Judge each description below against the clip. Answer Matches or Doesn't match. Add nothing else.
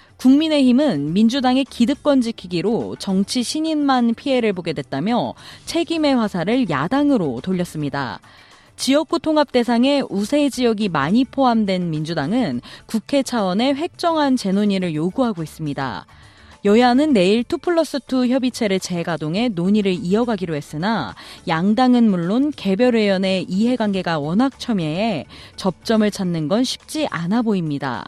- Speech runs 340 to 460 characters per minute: Doesn't match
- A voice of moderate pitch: Doesn't match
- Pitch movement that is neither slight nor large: Doesn't match